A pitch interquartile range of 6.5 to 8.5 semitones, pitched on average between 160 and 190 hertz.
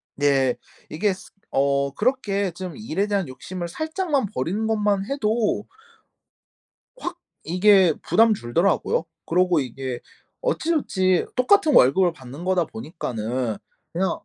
Yes: wide, 7.2 semitones; medium, 185 Hz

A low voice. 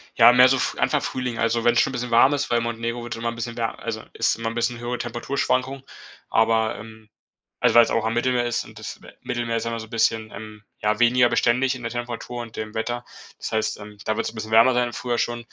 Yes: low, 120 Hz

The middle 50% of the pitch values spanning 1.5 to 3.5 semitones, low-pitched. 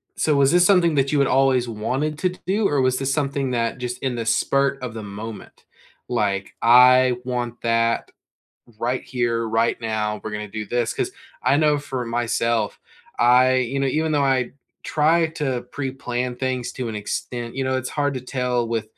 Yes: average, 3.0 semitones; low, 125 Hz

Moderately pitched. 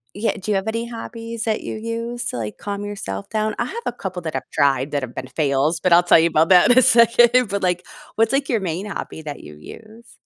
No: high, 205 Hz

